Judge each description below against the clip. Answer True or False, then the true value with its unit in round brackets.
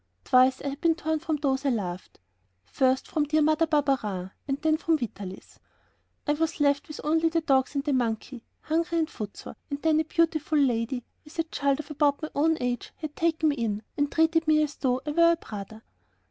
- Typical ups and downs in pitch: True (3.6 semitones)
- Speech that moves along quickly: True (210 wpm)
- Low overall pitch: False (295 Hz)